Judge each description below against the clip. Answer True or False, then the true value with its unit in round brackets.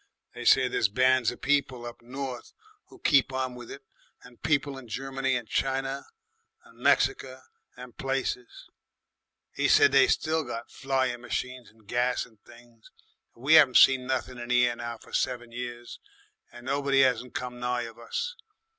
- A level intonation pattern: True (1.8 semitones)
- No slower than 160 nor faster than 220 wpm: True (170 wpm)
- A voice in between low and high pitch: False (125 Hz)